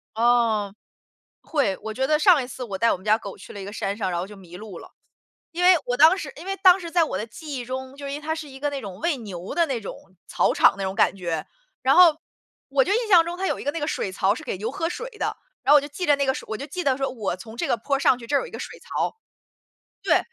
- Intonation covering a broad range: Yes, wide, 7.0 semitones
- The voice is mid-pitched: No, very high, 265 Hz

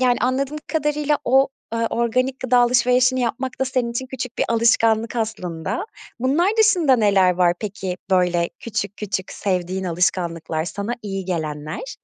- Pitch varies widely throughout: Yes, wide, 5.7 semitones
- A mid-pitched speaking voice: No, high, 230 Hz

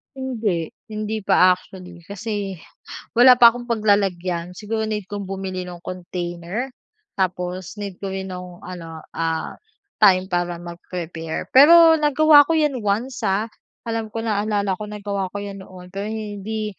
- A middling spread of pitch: Yes, average, 3.4 semitones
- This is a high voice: Yes, high, 200 Hz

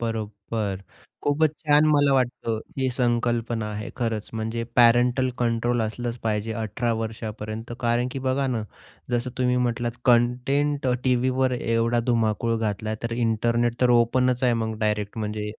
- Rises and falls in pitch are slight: Yes, narrow, 2.0 semitones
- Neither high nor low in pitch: No, low, 120 Hz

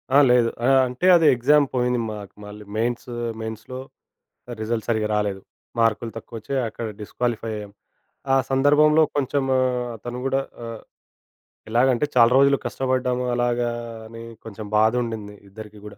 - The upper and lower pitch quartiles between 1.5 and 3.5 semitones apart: Yes, average, 2.9 semitones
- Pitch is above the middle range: No, low, 120 Hz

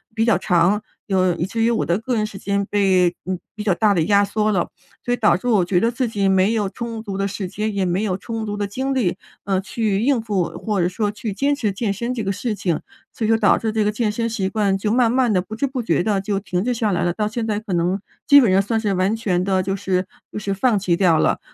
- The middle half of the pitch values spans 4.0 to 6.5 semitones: No, average, 2.9 semitones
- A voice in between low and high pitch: No, high, 205 Hz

